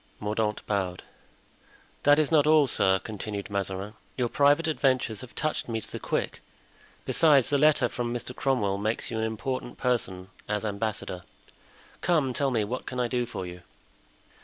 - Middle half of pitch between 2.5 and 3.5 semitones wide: No, average, 4.6 semitones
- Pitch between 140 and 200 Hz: No, low, 120 Hz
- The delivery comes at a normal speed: Yes, average, 165 wpm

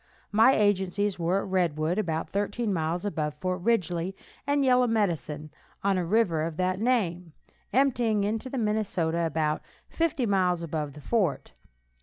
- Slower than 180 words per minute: Yes, average, 155 wpm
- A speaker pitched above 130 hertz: Yes, medium, 185 Hz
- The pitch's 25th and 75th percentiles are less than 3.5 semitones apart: No, average, 4.7 semitones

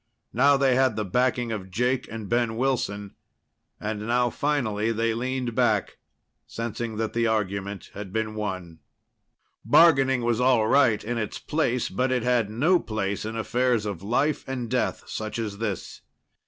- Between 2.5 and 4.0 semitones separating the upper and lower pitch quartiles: Yes, average, 3.0 semitones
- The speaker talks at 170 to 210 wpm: No, average, 160 wpm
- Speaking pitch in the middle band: No, low, 115 Hz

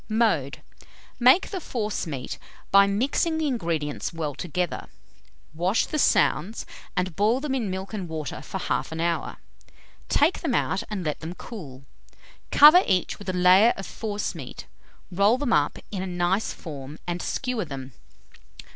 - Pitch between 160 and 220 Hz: Yes, high, 190 Hz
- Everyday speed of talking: Yes, average, 155 wpm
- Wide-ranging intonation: Yes, wide, 5.7 semitones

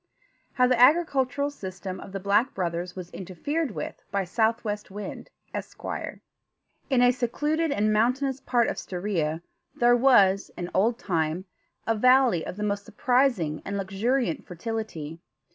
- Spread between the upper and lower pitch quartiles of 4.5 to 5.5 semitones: Yes, average, 5.1 semitones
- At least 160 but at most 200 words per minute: No, average, 145 wpm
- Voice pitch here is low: No, high, 210 Hz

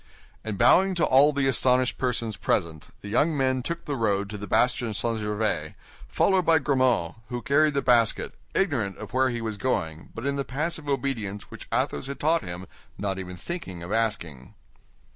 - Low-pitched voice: Yes, low, 120 Hz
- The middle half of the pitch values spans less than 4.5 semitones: No, wide, 5.5 semitones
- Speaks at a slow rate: No, average, 185 wpm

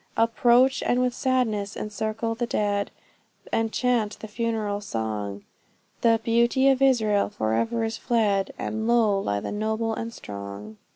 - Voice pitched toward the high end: Yes, high, 220 Hz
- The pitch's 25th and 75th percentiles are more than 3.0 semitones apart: No, average, 2.7 semitones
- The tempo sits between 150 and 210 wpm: No, average, 140 wpm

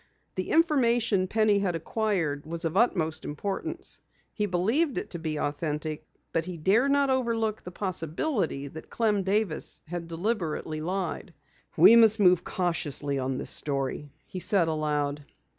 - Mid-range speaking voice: Yes, medium, 180 Hz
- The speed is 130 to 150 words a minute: Yes, average, 145 wpm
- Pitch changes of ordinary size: No, wide, 5.8 semitones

